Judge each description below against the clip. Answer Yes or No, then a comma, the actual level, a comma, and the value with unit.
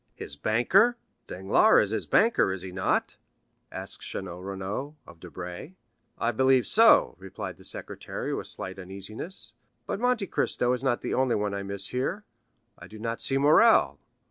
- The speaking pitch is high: No, low, 110 Hz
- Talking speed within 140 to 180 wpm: Yes, average, 165 wpm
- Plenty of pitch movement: Yes, wide, 6.4 semitones